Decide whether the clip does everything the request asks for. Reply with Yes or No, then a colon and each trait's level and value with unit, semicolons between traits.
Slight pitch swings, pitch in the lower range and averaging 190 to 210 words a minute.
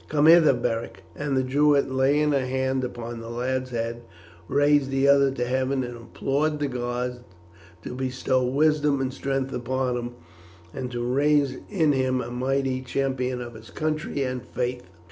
No: narrow, 2.2 semitones; low, 130 Hz; average, 165 wpm